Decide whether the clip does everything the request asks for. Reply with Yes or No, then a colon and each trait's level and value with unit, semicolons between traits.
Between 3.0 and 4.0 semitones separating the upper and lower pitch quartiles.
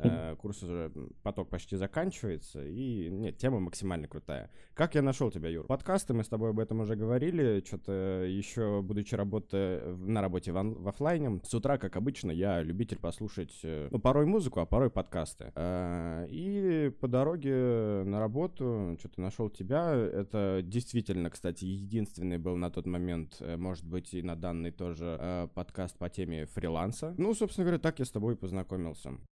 No: average, 5.2 semitones